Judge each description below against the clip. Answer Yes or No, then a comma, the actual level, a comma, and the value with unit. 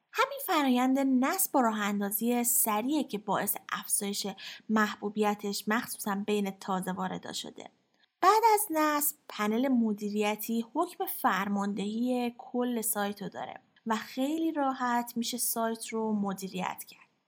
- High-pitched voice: Yes, high, 230 Hz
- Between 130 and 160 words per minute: No, average, 120 wpm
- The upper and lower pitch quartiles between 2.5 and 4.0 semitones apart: No, average, 4.5 semitones